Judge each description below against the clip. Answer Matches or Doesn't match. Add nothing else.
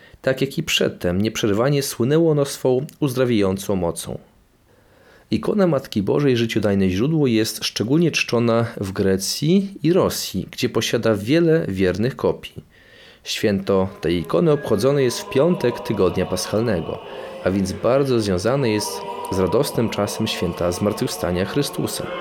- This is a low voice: Matches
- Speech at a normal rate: Matches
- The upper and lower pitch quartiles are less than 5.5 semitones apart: Doesn't match